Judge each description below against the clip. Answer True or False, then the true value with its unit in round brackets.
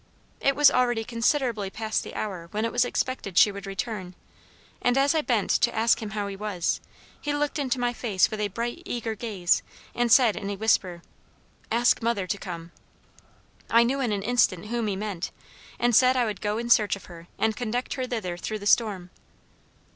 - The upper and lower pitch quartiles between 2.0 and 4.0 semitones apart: True (3.5 semitones)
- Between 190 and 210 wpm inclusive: True (200 wpm)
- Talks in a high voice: True (220 Hz)